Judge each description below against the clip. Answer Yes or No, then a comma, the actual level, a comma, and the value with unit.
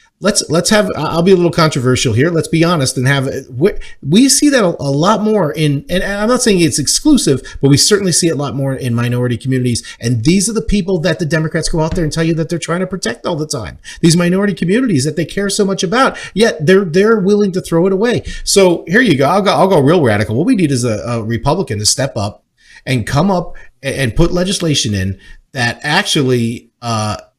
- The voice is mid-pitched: Yes, medium, 165 Hz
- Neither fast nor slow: No, fast, 235 wpm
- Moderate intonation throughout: No, wide, 6.3 semitones